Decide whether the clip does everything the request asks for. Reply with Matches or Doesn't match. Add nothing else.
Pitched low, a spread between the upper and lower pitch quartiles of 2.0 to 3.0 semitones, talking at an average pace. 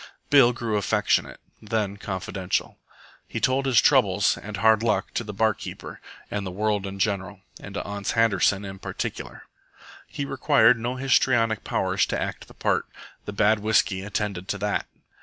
Matches